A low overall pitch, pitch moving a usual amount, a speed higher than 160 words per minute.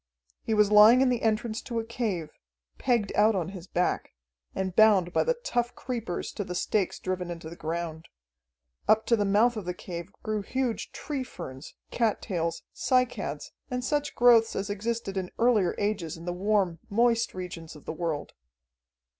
No: high, 205 Hz; average, 4.7 semitones; average, 175 wpm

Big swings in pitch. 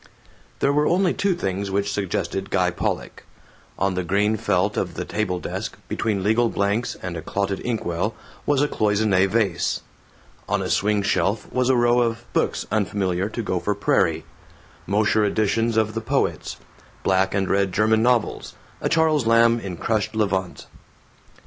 No: average, 3.0 semitones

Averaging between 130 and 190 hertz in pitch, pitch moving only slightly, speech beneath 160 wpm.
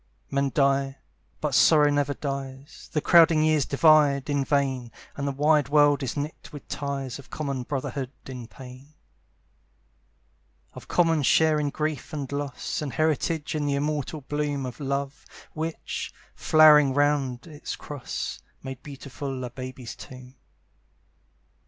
Yes: medium, 140 Hz; narrow, 2.0 semitones; average, 140 wpm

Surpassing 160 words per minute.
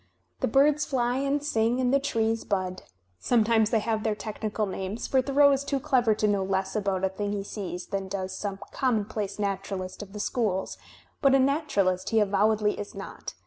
Yes: average, 190 wpm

